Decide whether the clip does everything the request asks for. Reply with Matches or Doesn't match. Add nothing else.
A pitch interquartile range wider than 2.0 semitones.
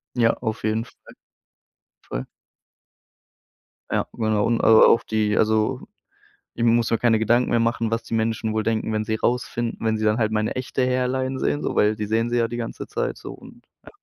Doesn't match